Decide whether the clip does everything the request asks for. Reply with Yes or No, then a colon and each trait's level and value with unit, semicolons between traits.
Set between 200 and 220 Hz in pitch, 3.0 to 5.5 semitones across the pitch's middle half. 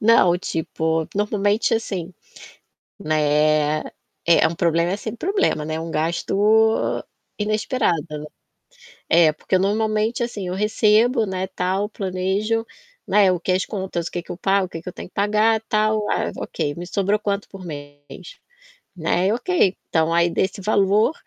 No: high, 190 Hz; average, 4.1 semitones